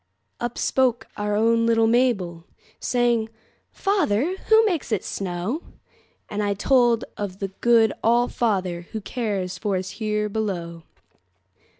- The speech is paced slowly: Yes, slow, 115 wpm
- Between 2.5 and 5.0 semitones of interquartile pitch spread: Yes, average, 3.5 semitones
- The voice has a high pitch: Yes, high, 220 Hz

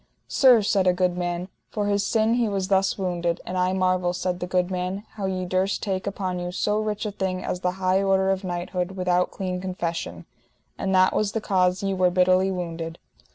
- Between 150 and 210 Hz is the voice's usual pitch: Yes, medium, 185 Hz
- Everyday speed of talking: No, fast, 210 wpm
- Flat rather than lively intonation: Yes, narrow, 1.4 semitones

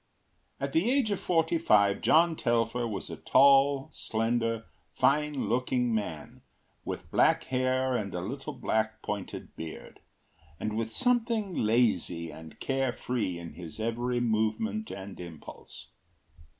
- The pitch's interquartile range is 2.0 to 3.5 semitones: No, average, 4.8 semitones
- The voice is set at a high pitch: No, low, 120 Hz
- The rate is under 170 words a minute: Yes, slow, 135 wpm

